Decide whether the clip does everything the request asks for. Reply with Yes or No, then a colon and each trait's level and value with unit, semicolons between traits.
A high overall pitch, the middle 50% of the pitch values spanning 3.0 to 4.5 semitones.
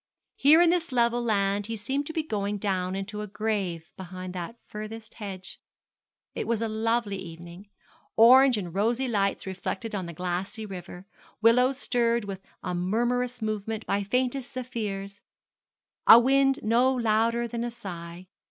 Yes: high, 215 Hz; average, 3.7 semitones